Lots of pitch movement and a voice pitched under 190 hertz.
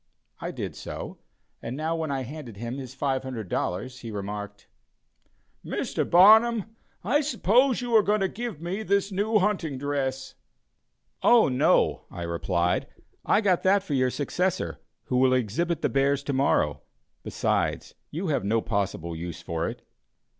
Yes: wide, 8.8 semitones; medium, 140 Hz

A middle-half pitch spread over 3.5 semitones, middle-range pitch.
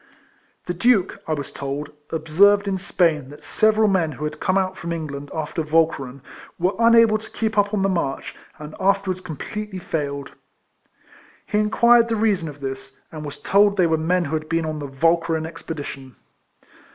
Yes: average, 4.8 semitones; medium, 165 Hz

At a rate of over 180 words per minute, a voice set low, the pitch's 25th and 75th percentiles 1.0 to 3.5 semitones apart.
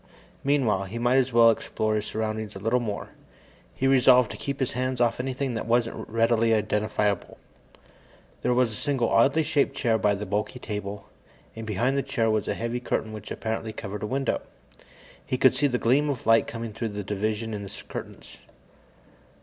Yes: average, 190 wpm; low, 115 Hz; average, 3.0 semitones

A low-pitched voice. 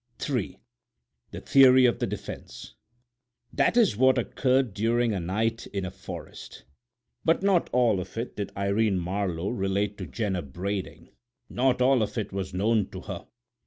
Yes: low, 105 Hz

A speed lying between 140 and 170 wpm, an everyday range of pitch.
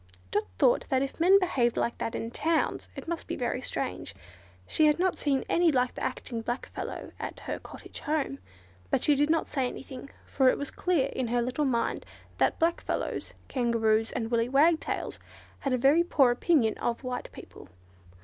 No: average, 195 wpm; average, 4.4 semitones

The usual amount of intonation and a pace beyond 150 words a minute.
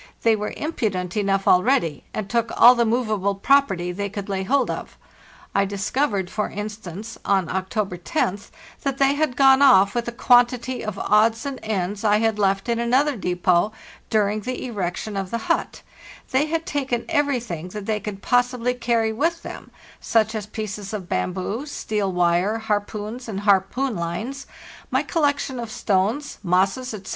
Yes: average, 4.1 semitones; average, 170 wpm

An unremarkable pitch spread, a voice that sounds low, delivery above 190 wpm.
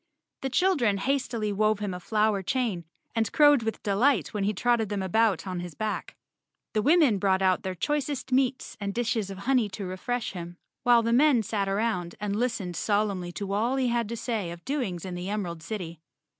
No: average, 4.1 semitones; high, 215 Hz; average, 200 wpm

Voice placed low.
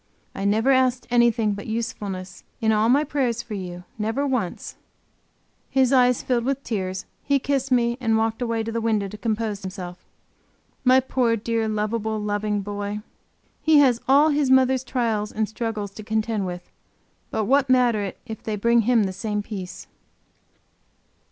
No: high, 225 Hz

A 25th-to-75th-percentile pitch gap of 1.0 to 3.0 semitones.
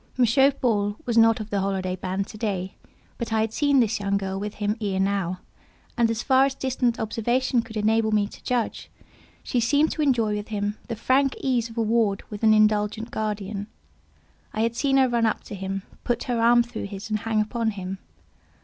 Yes: narrow, 2.6 semitones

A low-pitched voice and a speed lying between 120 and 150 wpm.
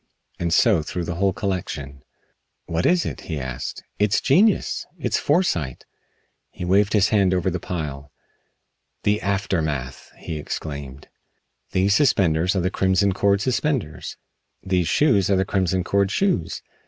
Yes: very low, 95 Hz; average, 140 wpm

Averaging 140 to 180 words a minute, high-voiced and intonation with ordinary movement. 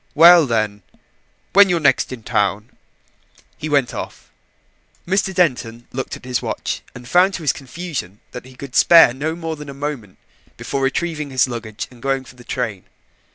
No: average, 175 wpm; low, 135 Hz; average, 5.0 semitones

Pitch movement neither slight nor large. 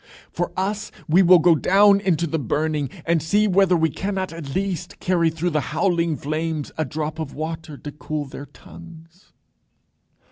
Yes: average, 3.0 semitones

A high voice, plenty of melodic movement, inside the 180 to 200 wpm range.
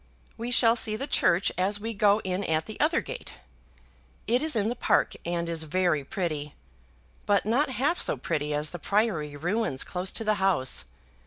Yes: high, 195 Hz; wide, 5.7 semitones; average, 185 wpm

